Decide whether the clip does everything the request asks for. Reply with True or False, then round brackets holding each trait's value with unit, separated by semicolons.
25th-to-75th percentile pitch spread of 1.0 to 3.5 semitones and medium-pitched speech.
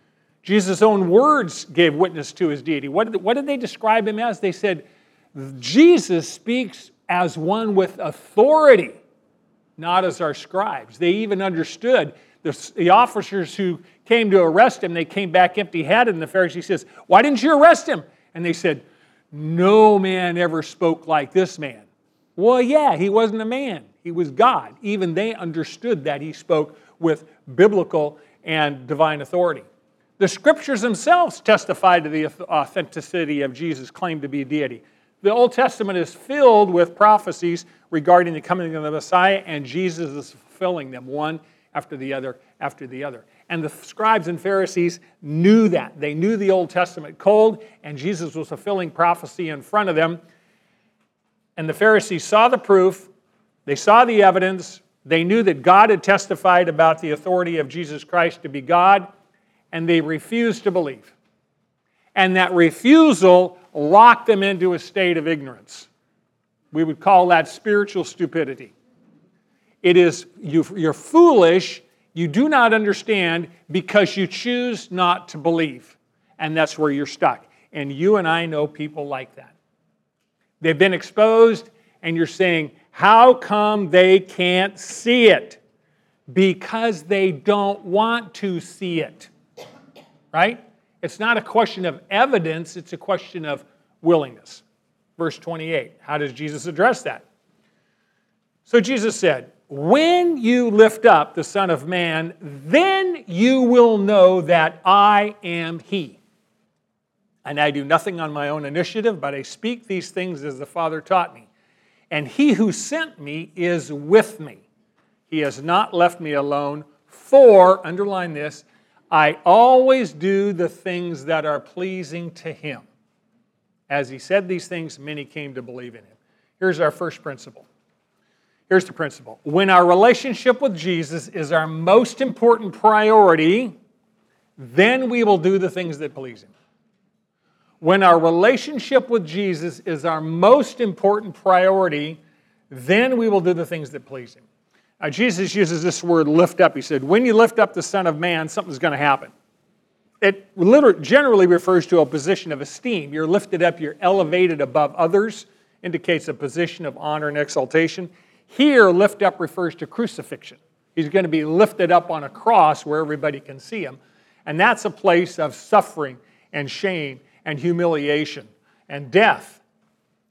False (4.7 semitones; 180 Hz)